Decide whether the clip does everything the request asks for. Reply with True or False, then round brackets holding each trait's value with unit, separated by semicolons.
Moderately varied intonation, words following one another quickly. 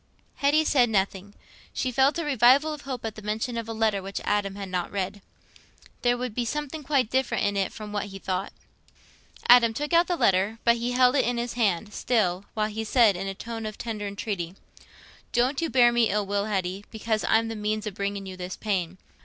True (3.6 semitones; 220 wpm)